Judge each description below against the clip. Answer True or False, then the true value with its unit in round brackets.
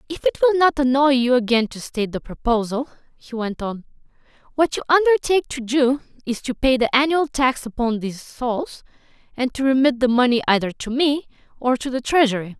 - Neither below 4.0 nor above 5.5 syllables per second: False (5.8 syllables/s)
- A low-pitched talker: False (255 Hz)